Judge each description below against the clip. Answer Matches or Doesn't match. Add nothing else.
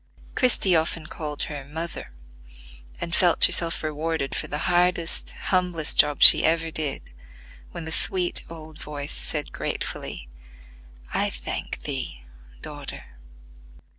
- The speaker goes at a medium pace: Doesn't match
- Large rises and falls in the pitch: Doesn't match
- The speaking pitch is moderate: Matches